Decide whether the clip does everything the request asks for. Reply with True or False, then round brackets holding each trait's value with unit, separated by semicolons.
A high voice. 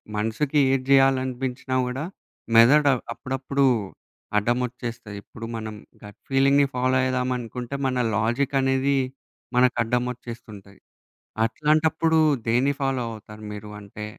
False (125 Hz)